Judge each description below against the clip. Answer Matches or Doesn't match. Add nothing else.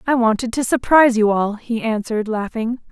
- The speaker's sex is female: Matches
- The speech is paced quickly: Doesn't match